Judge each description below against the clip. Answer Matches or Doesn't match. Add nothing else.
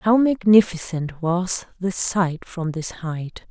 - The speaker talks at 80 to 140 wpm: Matches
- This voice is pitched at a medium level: Matches